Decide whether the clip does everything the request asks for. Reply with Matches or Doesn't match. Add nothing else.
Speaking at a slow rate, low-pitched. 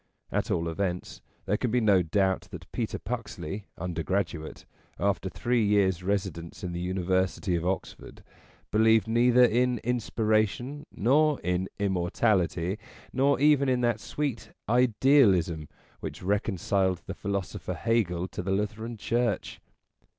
Matches